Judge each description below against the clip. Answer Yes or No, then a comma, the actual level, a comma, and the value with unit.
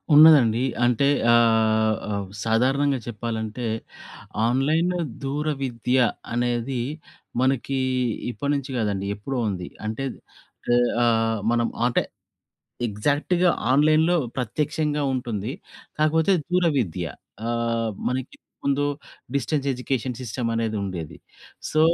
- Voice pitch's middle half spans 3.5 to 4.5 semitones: Yes, average, 4.1 semitones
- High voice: No, low, 125 Hz